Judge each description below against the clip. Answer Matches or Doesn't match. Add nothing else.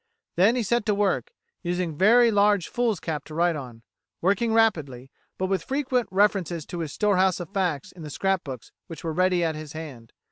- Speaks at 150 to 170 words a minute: Doesn't match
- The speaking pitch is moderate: Matches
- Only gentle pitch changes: Doesn't match